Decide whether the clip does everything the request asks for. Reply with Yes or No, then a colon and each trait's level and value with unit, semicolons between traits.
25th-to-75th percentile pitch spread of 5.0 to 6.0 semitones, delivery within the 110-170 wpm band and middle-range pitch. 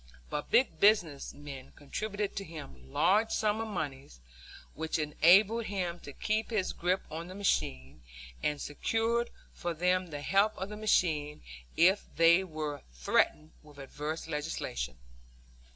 Yes: wide, 5.6 semitones; average, 140 wpm; medium, 170 Hz